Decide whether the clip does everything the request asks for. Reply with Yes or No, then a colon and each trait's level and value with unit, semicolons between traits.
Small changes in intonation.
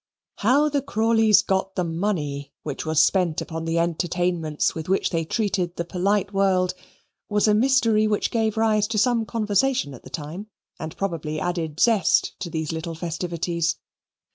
No: average, 4.7 semitones